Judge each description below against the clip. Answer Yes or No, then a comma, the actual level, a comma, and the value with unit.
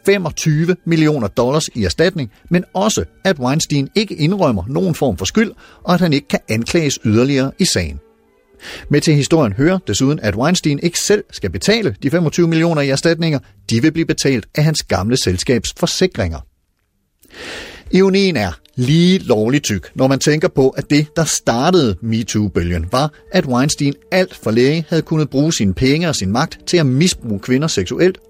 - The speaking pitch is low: No, medium, 145 Hz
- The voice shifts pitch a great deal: Yes, wide, 6.9 semitones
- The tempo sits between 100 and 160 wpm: No, average, 175 wpm